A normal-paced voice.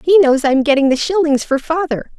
No: fast, 220 wpm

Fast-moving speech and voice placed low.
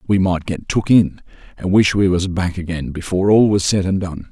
Yes: fast, 235 wpm; very low, 95 Hz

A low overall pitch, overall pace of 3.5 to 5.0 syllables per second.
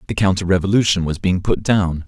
No: very low, 95 Hz; 5.8 syllables/s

